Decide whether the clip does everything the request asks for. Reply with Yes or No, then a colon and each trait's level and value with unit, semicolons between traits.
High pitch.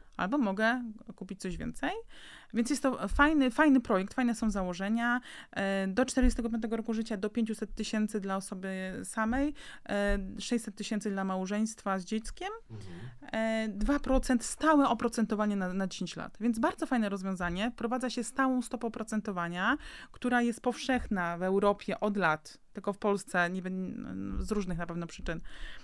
Yes: high, 220 Hz